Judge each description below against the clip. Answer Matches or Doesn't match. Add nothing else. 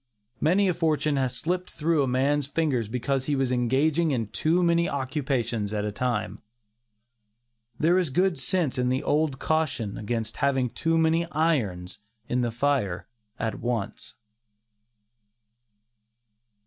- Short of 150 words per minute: Matches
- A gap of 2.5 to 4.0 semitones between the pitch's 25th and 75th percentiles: Doesn't match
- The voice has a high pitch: Doesn't match